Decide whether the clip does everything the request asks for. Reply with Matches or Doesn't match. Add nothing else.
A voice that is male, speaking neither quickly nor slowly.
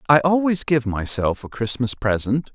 Matches